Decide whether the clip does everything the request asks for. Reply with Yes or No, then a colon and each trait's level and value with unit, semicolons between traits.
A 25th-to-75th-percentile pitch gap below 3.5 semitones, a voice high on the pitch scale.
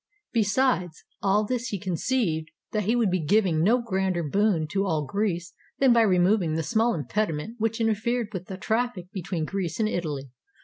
No: average, 4.5 semitones; high, 195 Hz